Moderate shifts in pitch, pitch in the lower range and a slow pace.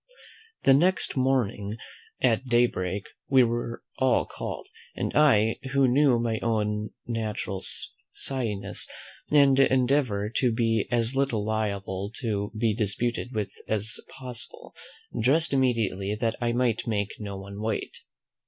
Yes: average, 3.5 semitones; low, 115 Hz; slow, 130 wpm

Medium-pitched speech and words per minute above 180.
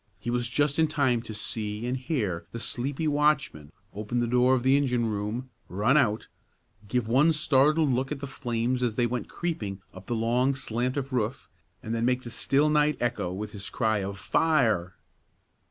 No: low, 125 Hz; average, 190 wpm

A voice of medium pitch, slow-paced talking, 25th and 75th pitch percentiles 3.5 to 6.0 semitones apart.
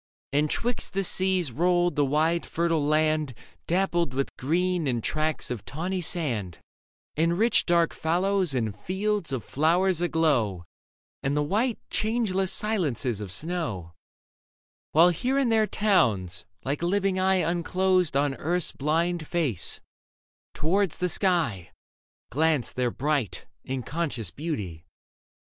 Yes: medium, 165 Hz; slow, 130 wpm; average, 5.1 semitones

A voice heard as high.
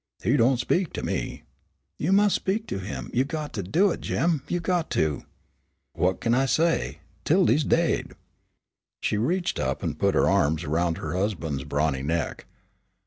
No: low, 120 Hz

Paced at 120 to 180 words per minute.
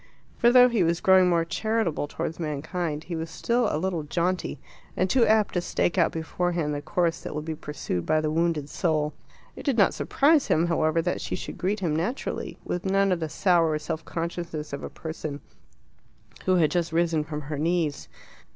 No: average, 195 wpm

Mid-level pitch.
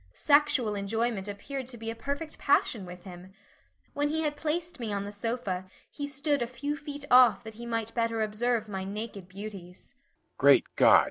No: high, 230 Hz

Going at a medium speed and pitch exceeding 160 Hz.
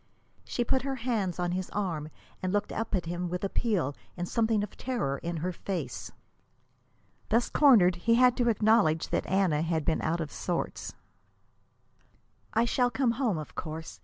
Yes: average, 170 wpm; high, 190 Hz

